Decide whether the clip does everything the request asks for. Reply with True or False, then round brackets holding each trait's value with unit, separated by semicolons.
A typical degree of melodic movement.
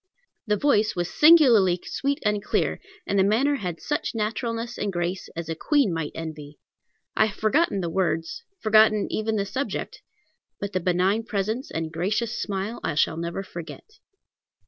True (4.7 semitones)